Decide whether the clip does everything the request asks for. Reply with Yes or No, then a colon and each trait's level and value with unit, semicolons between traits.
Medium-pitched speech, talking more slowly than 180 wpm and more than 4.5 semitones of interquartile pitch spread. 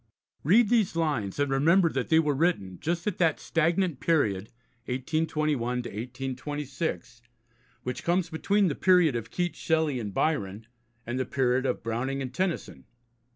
Yes: medium, 145 Hz; average, 150 wpm; average, 5.1 semitones